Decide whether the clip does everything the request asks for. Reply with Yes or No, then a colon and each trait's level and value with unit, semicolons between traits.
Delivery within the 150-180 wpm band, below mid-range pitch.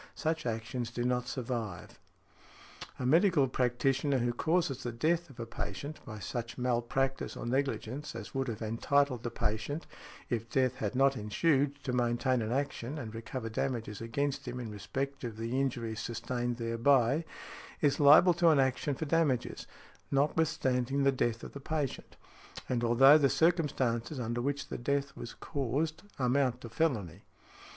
Yes: average, 160 wpm; low, 130 Hz